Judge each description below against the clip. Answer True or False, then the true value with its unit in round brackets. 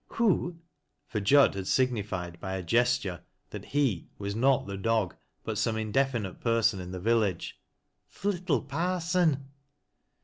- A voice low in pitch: True (115 Hz)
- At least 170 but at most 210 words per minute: False (150 wpm)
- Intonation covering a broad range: True (6.1 semitones)